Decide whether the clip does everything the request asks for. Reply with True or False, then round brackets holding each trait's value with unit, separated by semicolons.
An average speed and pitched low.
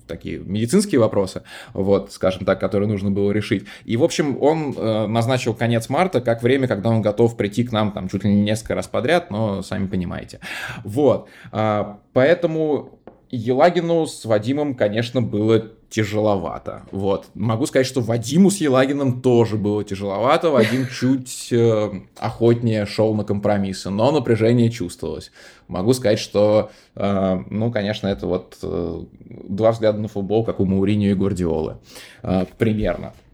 True (145 wpm; 110 Hz)